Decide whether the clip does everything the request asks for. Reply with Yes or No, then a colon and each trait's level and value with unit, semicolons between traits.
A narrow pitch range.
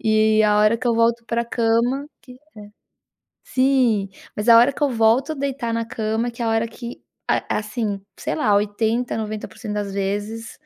Yes: narrow, 2.1 semitones